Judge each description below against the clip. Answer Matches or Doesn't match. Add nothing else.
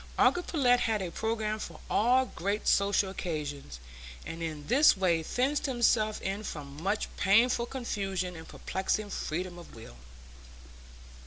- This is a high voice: Matches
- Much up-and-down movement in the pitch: Matches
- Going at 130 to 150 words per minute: Matches